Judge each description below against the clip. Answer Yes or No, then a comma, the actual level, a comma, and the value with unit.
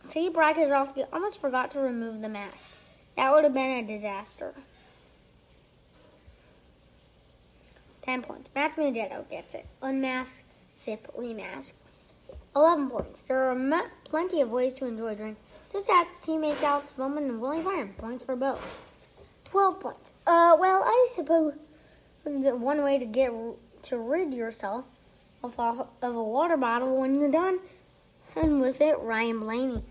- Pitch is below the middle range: No, very high, 265 Hz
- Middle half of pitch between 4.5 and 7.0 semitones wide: Yes, average, 4.8 semitones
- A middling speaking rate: Yes, average, 150 wpm